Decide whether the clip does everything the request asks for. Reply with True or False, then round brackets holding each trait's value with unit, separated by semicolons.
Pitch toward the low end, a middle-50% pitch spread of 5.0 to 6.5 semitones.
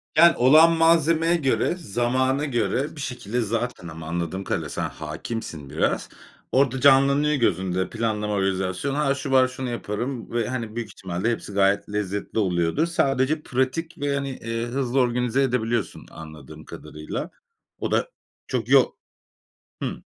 True (120 Hz; 5.5 semitones)